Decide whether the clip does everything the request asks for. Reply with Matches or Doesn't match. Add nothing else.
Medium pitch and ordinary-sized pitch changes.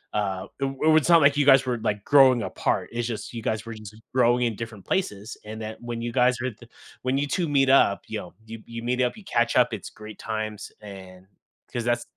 Doesn't match